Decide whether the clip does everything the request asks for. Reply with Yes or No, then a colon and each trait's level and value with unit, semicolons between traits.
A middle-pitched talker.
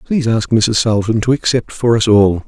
No: low, 110 Hz